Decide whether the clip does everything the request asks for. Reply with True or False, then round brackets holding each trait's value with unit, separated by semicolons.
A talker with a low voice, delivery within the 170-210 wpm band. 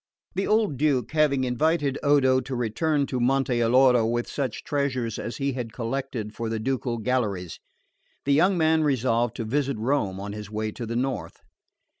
True (130 Hz; 175 wpm)